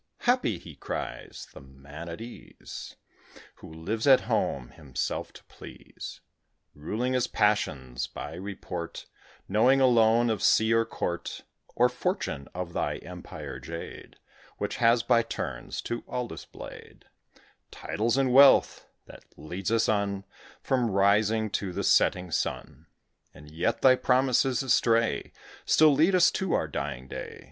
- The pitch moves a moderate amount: No, wide, 6.8 semitones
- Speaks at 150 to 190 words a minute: No, slow, 135 wpm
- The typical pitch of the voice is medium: No, low, 110 Hz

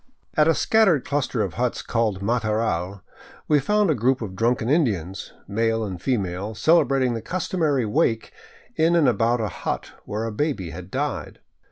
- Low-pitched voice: Yes, low, 115 Hz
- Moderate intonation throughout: No, wide, 5.7 semitones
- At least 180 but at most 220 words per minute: No, average, 165 wpm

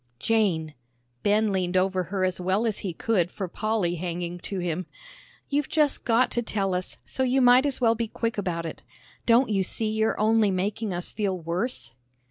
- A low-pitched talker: No, high, 200 Hz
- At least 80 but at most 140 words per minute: No, average, 190 wpm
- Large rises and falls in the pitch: No, average, 4.0 semitones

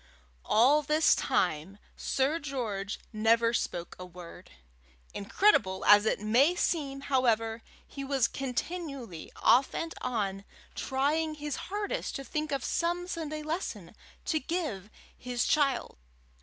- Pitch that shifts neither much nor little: No, wide, 6.1 semitones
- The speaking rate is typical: No, slow, 125 wpm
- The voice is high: Yes, very high, 270 Hz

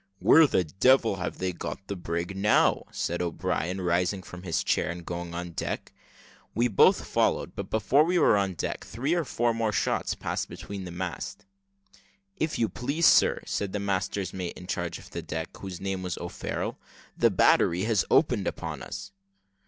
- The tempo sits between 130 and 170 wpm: No, average, 185 wpm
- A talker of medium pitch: No, very low, 95 Hz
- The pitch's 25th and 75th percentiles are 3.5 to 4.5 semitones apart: Yes, average, 3.9 semitones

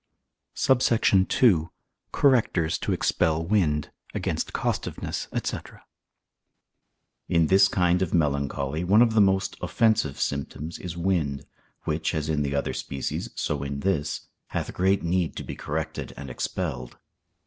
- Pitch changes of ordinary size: Yes, average, 4.5 semitones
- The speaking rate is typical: No, slow, 130 wpm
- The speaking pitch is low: Yes, very low, 80 Hz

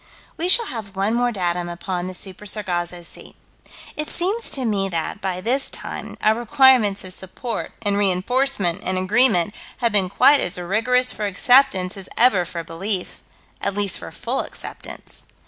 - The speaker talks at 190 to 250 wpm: No, average, 165 wpm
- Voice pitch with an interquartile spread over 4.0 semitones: Yes, average, 5.1 semitones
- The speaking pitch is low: No, high, 200 Hz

